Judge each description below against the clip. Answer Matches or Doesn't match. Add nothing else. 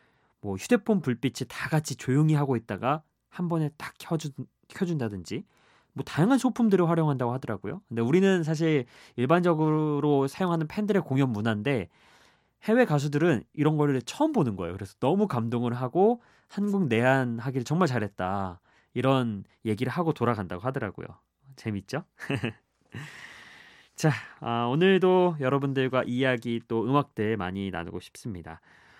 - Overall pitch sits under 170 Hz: Matches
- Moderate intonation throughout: Doesn't match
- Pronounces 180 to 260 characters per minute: Doesn't match